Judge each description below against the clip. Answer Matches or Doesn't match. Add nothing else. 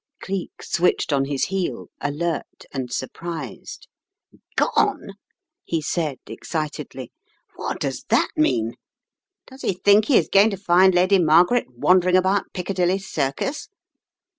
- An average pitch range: Matches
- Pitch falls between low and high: Matches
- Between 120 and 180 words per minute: Matches